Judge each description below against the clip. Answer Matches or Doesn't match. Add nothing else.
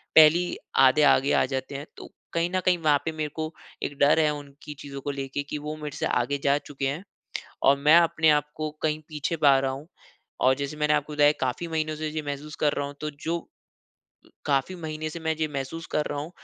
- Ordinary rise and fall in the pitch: Doesn't match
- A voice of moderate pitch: Matches